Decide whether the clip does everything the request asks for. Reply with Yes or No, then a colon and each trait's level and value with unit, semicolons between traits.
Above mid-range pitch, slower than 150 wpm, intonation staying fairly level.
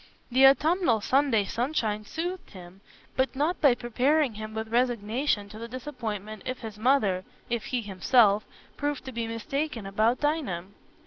No: high, 235 Hz; average, 140 wpm; average, 4.5 semitones